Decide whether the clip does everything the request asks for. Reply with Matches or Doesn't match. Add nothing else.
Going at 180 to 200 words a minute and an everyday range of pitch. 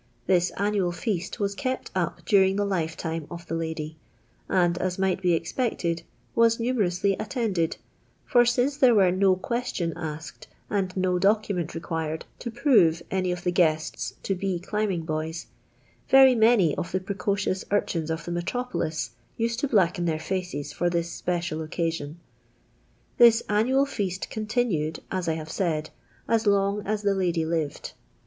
Doesn't match